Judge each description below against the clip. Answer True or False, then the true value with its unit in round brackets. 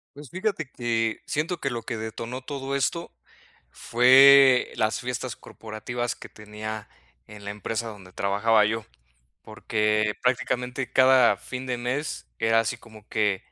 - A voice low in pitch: True (115 Hz)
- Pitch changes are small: False (3.2 semitones)